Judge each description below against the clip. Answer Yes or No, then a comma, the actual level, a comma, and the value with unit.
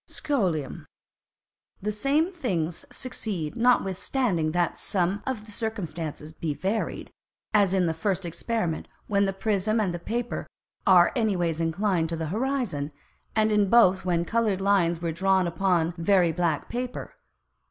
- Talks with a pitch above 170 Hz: Yes, high, 190 Hz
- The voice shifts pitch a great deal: No, average, 4.5 semitones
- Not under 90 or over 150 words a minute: Yes, average, 140 wpm